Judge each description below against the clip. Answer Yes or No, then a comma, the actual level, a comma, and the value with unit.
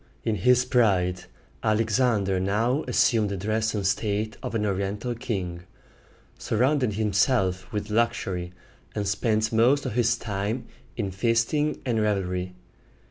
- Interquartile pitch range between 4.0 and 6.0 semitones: No, average, 3.2 semitones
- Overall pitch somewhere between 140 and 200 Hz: No, low, 110 Hz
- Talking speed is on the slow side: Yes, slow, 130 wpm